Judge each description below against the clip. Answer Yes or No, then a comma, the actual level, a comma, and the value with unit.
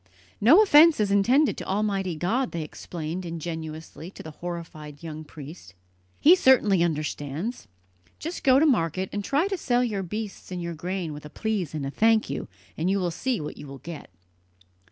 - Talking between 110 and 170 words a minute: No, average, 185 wpm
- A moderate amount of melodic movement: No, wide, 6.1 semitones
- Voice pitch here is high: No, medium, 180 Hz